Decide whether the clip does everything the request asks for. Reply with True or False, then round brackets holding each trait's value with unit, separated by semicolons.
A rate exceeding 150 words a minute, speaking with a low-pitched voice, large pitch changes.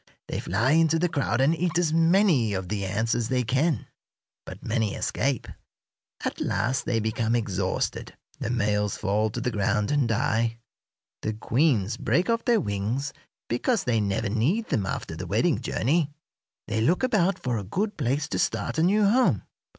True (175 wpm; 125 Hz; 7.1 semitones)